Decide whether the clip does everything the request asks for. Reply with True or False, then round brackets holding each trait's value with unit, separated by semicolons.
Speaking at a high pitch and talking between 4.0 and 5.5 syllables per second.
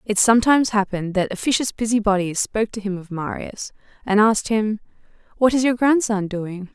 False (215 Hz; 5.8 syllables/s)